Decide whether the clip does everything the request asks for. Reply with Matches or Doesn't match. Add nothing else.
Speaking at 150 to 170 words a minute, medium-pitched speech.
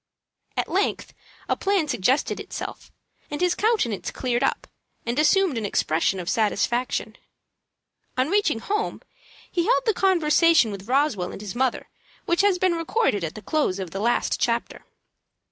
Doesn't match